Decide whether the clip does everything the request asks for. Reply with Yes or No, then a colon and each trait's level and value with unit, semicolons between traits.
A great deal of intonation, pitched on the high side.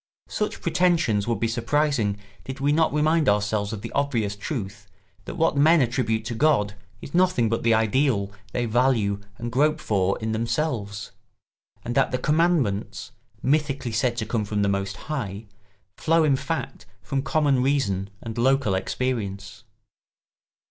No: wide, 5.7 semitones; low, 120 Hz